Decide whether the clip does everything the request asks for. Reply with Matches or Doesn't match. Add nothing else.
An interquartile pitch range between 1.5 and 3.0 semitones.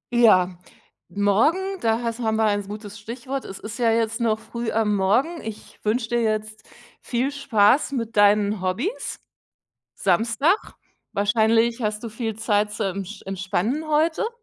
Matches